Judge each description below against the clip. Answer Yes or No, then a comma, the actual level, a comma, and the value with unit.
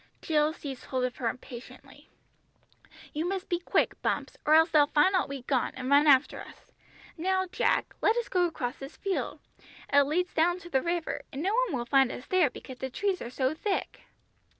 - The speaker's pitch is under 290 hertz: No, very high, 300 Hz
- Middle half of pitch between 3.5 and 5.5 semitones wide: Yes, average, 5.2 semitones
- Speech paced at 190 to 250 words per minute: Yes, average, 200 wpm